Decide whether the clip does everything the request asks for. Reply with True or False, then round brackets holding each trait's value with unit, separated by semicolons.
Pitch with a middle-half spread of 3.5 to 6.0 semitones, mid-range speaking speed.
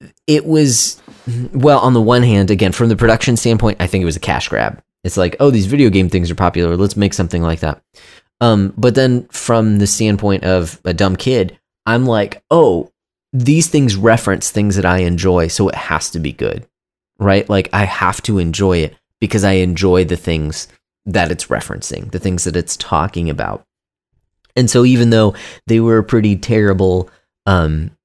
True (4.0 semitones; 195 wpm)